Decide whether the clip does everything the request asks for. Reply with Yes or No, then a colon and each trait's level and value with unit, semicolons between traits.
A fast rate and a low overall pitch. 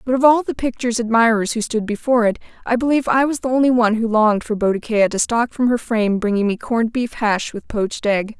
No: fast, 245 wpm; high, 230 Hz